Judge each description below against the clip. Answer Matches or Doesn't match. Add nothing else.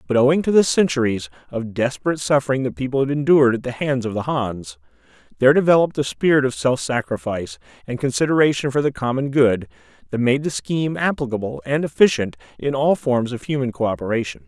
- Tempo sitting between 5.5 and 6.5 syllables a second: Matches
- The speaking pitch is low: Matches